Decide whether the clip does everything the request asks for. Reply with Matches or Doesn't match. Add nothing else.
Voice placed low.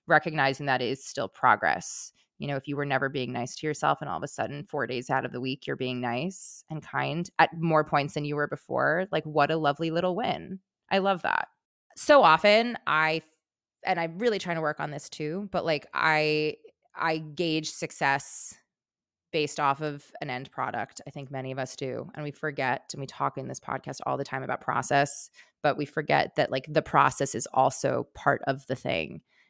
Doesn't match